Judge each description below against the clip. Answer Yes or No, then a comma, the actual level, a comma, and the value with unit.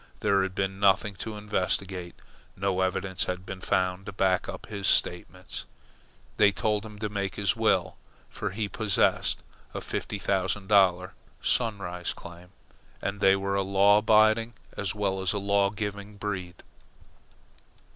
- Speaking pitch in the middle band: No, low, 100 Hz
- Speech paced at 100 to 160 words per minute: Yes, average, 150 wpm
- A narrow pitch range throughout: Yes, narrow, 1.7 semitones